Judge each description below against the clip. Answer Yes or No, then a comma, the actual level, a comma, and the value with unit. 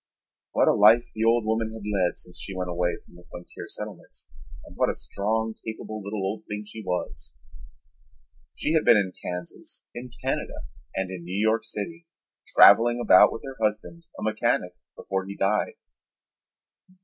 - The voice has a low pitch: Yes, low, 105 Hz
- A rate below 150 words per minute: No, average, 170 wpm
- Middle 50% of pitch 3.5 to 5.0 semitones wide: No, average, 3.1 semitones